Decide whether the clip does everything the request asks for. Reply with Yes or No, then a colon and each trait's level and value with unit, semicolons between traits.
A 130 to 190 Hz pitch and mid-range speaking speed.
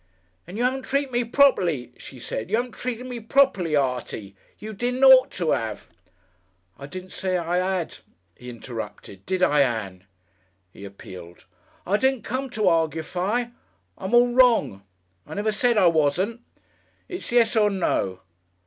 Yes: medium, 185 Hz; average, 160 wpm